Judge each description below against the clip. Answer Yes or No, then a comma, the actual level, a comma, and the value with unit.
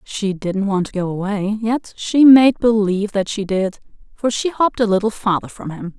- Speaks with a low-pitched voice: No, high, 210 Hz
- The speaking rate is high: Yes, fast, 210 wpm